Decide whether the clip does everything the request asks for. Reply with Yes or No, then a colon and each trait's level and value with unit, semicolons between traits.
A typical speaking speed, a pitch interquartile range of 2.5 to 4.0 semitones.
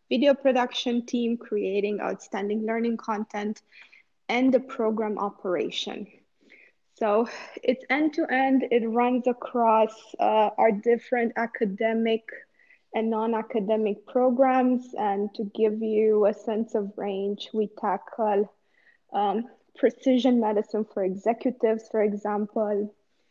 No: slow, 115 wpm; average, 2.8 semitones